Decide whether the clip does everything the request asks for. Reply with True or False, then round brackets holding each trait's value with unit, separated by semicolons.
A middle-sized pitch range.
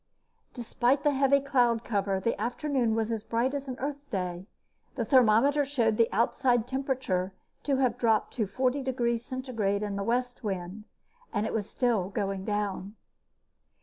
True (4.1 semitones)